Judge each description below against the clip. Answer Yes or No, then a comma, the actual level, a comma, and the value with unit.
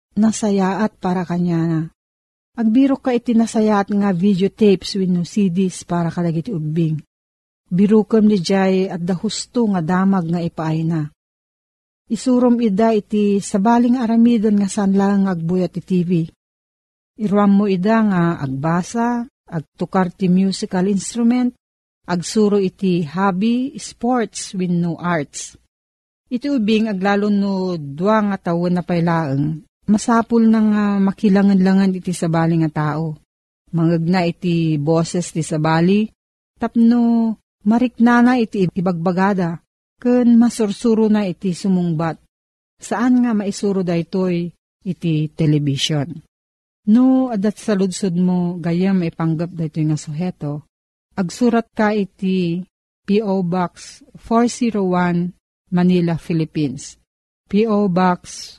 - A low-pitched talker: No, high, 190 Hz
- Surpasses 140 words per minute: No, average, 120 wpm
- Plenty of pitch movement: No, average, 4.2 semitones